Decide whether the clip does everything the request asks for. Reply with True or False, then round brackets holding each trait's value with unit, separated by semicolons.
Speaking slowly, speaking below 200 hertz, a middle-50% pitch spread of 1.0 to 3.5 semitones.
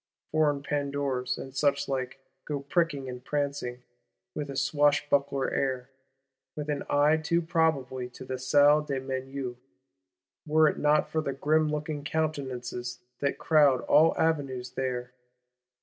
True (130 wpm; 140 Hz; 2.5 semitones)